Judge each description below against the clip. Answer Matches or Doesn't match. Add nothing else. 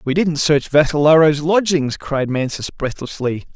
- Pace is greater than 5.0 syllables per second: Doesn't match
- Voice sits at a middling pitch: Matches